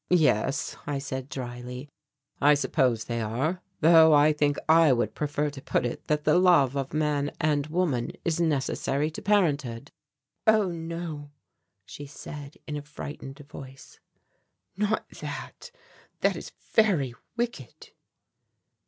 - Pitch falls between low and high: Yes, medium, 145 Hz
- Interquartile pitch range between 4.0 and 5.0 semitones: No, average, 3.3 semitones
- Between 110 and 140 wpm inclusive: Yes, slow, 135 wpm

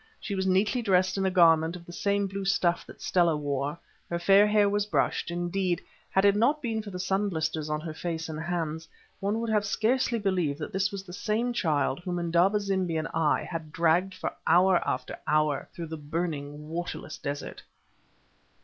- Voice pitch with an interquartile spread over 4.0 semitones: No, average, 3.7 semitones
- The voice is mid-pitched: Yes, medium, 175 Hz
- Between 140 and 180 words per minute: No, average, 195 wpm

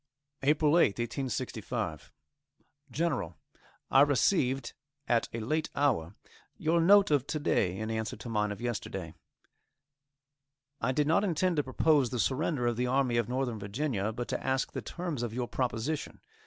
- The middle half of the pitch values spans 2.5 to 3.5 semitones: No, average, 4.6 semitones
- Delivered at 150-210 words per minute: Yes, average, 155 wpm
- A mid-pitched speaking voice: No, low, 130 Hz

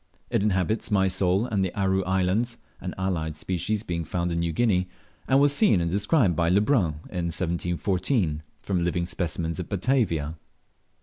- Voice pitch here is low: Yes, very low, 90 Hz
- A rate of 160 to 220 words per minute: Yes, average, 165 wpm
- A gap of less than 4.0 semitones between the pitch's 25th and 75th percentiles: Yes, average, 3.2 semitones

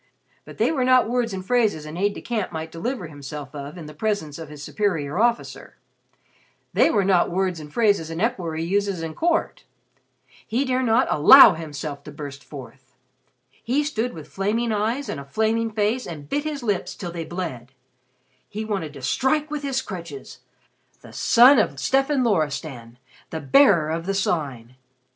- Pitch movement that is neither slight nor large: No, wide, 7.5 semitones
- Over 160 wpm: Yes, average, 175 wpm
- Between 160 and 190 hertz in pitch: Yes, medium, 185 Hz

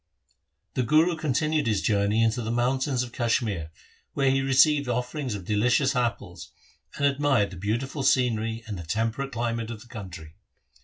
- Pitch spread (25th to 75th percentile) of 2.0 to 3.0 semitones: No, average, 3.8 semitones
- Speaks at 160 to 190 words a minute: Yes, average, 165 wpm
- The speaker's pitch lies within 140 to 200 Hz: No, low, 120 Hz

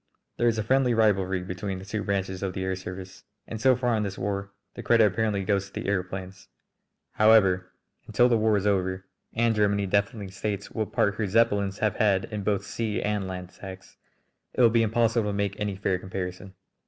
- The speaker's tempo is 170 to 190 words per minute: No, fast, 205 wpm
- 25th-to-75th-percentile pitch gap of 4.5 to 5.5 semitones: No, narrow, 2.5 semitones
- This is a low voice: Yes, low, 100 Hz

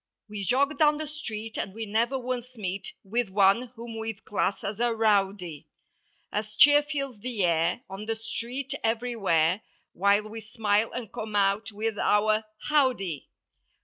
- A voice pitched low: No, high, 220 Hz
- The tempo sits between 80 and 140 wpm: No, average, 150 wpm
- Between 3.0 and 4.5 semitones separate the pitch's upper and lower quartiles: Yes, average, 3.3 semitones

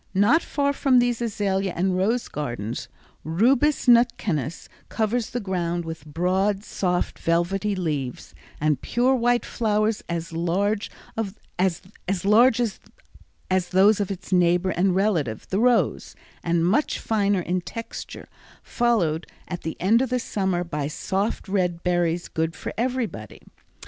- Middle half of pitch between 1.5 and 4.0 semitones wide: No, average, 4.7 semitones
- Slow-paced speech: Yes, slow, 130 wpm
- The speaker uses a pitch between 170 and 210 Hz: Yes, high, 190 Hz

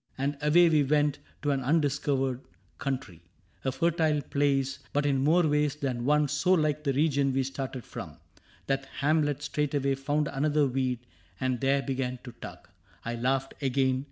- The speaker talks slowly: No, average, 170 wpm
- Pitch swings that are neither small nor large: No, narrow, 2.0 semitones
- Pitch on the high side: No, medium, 140 Hz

